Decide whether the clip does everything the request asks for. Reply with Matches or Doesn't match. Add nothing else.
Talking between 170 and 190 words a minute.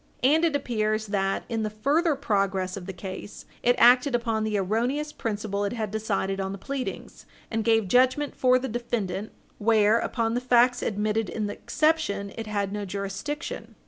Matches